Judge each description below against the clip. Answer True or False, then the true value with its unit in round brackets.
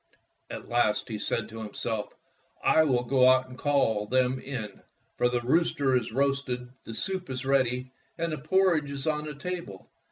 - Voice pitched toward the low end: True (130 Hz)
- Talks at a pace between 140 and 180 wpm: False (190 wpm)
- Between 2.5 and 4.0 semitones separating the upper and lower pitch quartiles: True (3.2 semitones)